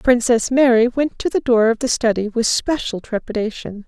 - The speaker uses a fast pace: No, average, 185 wpm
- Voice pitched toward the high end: Yes, high, 235 Hz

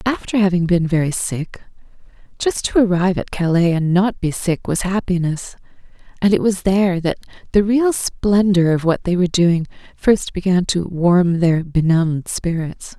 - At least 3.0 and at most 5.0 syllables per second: Yes, 4.8 syllables/s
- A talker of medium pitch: Yes, medium, 180 Hz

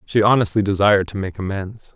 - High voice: No, low, 100 Hz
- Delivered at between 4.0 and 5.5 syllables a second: No, 6.0 syllables/s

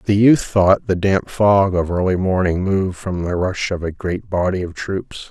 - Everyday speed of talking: No, fast, 215 wpm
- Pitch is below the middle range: Yes, very low, 95 Hz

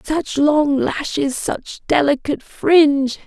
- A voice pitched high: Yes, very high, 280 Hz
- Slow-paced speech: Yes, slow, 110 wpm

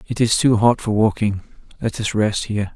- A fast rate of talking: Yes, fast, 220 wpm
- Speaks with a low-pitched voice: Yes, low, 110 Hz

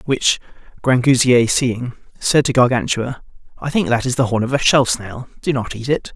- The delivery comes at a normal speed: Yes, average, 195 wpm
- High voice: No, low, 125 Hz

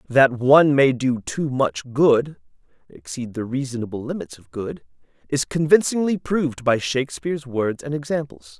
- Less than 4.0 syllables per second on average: Yes, 3.8 syllables/s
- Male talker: Yes, male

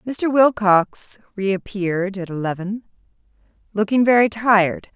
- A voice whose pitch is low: No, high, 205 Hz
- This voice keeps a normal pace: No, slow, 95 wpm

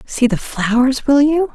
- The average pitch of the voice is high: Yes, very high, 265 Hz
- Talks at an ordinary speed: Yes, average, 195 wpm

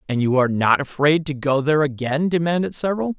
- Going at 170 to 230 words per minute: Yes, fast, 205 wpm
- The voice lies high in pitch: No, medium, 150 Hz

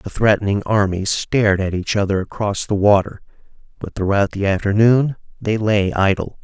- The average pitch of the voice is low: Yes, low, 105 Hz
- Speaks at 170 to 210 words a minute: No, average, 160 wpm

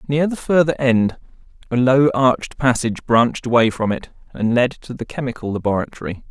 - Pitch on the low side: Yes, low, 125 Hz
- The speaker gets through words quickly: No, average, 170 wpm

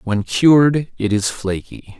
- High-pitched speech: No, low, 115 Hz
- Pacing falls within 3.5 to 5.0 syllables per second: Yes, 3.8 syllables/s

